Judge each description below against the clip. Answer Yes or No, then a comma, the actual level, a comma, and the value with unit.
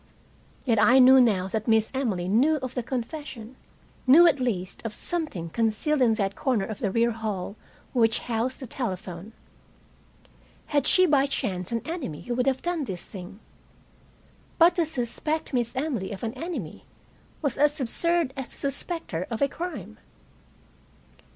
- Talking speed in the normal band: Yes, average, 165 wpm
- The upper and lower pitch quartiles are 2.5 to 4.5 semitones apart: No, average, 5.0 semitones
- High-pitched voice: Yes, high, 245 Hz